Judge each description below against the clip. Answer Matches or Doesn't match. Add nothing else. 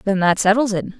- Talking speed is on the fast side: Matches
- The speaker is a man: Doesn't match